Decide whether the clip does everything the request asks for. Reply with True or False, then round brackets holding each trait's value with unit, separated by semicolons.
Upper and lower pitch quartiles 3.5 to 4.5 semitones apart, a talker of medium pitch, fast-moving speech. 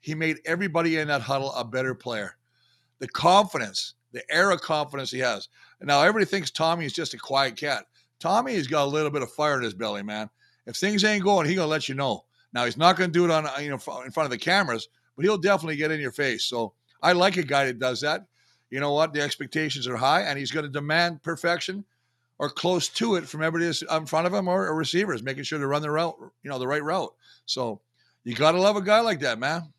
True (4.2 semitones; 150 Hz; 245 wpm)